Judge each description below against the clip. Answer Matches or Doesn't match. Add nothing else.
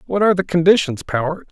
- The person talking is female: Doesn't match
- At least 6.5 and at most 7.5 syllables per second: Matches